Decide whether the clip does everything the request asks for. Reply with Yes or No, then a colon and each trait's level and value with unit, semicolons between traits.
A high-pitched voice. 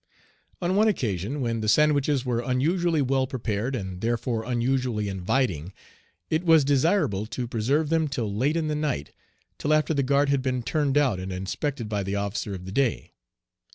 No: low, 130 Hz